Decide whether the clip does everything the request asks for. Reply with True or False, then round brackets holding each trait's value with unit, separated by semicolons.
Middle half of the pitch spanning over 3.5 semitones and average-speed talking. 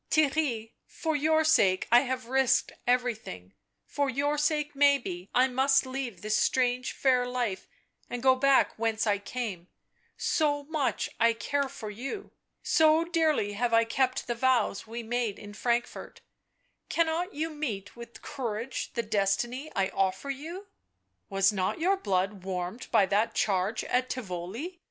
True (5.2 semitones; 160 wpm)